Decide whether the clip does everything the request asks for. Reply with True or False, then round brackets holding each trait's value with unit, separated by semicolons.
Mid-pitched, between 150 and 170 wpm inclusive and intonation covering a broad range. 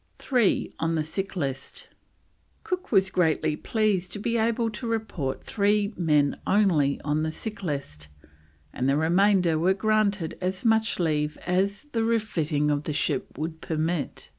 True (180 Hz; 155 wpm; 5.7 semitones)